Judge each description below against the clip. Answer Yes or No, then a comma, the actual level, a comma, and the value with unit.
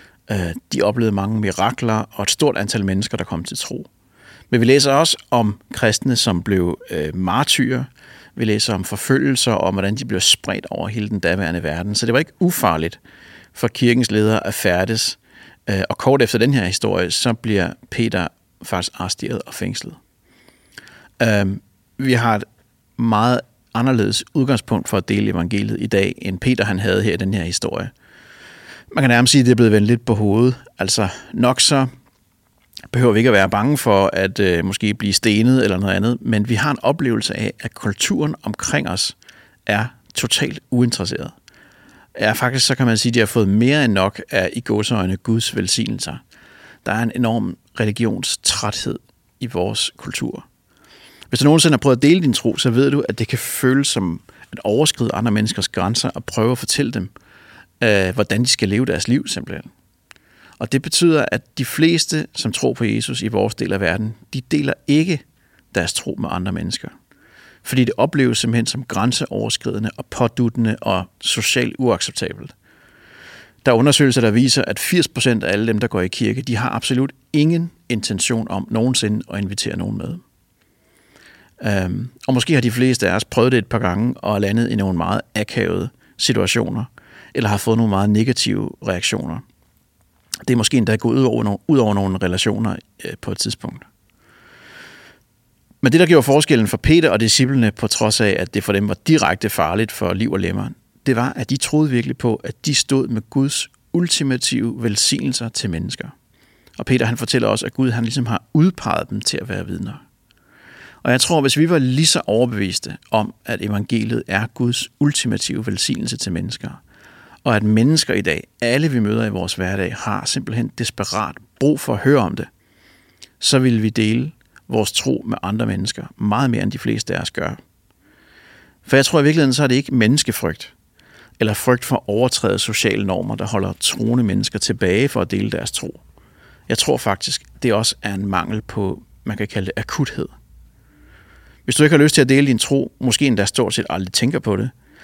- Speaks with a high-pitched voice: No, low, 115 Hz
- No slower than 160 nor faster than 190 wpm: Yes, average, 185 wpm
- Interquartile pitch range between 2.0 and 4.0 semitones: Yes, average, 3.7 semitones